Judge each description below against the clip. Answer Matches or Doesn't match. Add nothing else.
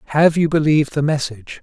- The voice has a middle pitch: Matches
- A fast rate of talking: Doesn't match